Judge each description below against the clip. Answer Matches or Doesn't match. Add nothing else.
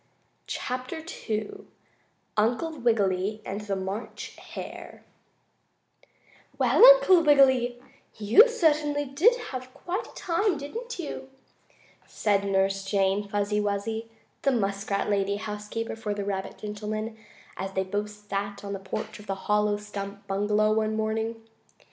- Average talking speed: Doesn't match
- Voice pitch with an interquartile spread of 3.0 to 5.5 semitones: Matches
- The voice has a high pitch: Matches